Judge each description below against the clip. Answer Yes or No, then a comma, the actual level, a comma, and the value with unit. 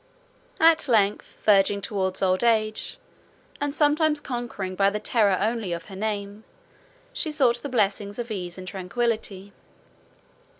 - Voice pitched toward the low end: No, high, 210 Hz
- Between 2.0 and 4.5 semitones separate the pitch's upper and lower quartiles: Yes, average, 3.6 semitones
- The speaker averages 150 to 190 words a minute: No, slow, 135 wpm